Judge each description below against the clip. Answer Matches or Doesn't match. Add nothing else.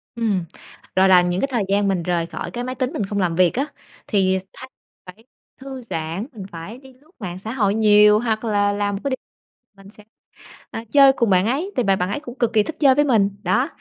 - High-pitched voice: Matches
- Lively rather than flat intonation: Doesn't match